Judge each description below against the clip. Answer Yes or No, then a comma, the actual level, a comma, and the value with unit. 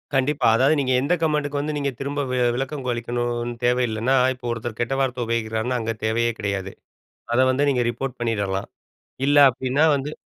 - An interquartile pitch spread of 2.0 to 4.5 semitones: Yes, average, 3.0 semitones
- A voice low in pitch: Yes, low, 125 Hz